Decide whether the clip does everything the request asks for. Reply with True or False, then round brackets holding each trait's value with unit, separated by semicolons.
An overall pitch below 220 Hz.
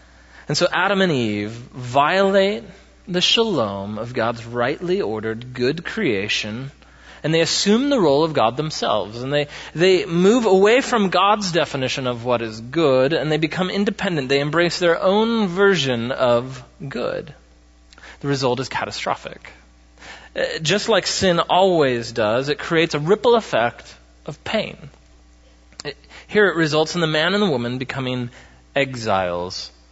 True (140 Hz)